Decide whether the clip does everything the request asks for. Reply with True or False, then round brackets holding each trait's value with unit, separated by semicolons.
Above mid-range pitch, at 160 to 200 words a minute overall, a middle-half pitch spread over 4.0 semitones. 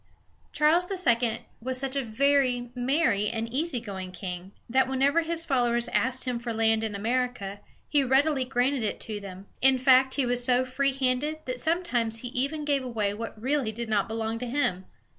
False (250 Hz; 185 wpm; 3.4 semitones)